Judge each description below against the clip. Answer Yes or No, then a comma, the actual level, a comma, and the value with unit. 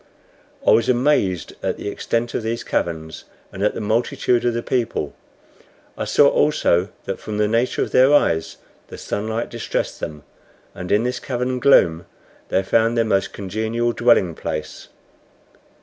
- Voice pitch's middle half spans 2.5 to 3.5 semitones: No, average, 4.0 semitones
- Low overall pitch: Yes, low, 110 Hz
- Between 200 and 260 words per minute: No, average, 160 wpm